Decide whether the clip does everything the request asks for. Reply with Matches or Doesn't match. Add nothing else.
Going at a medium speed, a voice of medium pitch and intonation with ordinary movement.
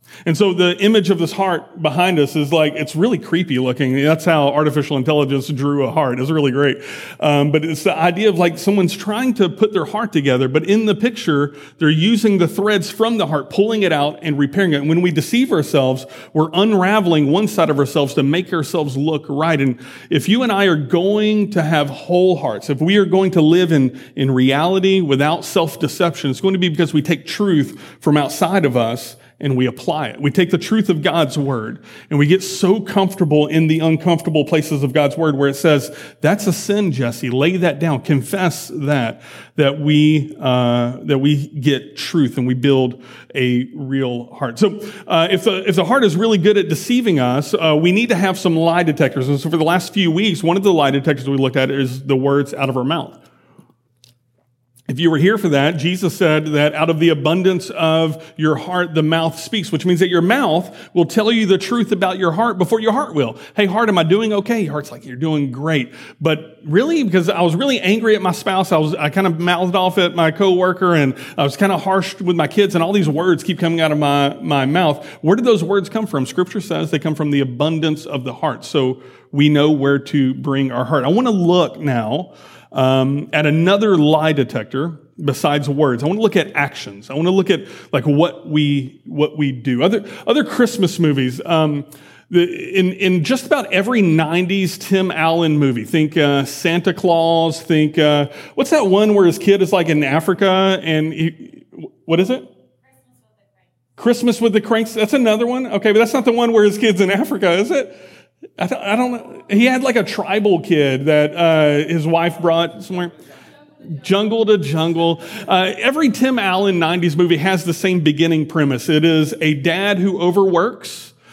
Doesn't match